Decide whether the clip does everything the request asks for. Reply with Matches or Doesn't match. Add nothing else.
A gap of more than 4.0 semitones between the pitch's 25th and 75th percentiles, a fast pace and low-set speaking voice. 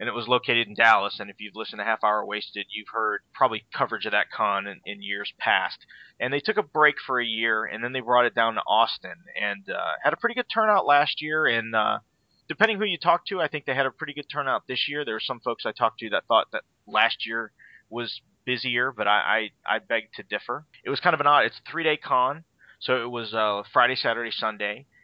Matches